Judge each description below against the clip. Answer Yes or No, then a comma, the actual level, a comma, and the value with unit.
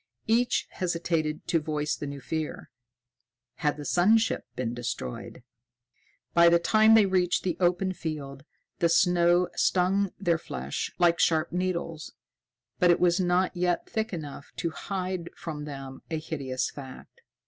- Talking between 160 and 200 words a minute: No, average, 150 wpm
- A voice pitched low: No, medium, 170 Hz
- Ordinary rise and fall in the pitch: Yes, average, 3.2 semitones